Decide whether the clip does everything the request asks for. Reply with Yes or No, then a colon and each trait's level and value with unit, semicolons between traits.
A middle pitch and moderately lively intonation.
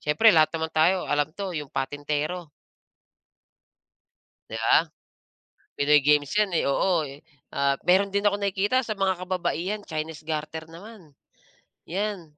Yes: medium, 165 Hz; average, 4.6 semitones